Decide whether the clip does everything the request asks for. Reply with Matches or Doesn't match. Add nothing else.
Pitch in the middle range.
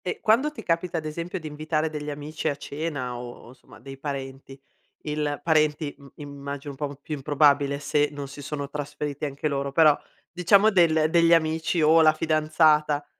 Matches